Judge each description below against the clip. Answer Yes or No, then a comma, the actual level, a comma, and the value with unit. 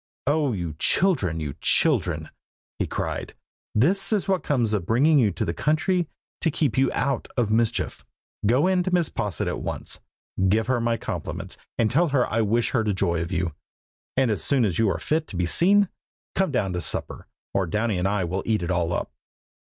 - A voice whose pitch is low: Yes, low, 115 Hz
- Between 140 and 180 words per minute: No, average, 200 wpm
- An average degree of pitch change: No, wide, 7.8 semitones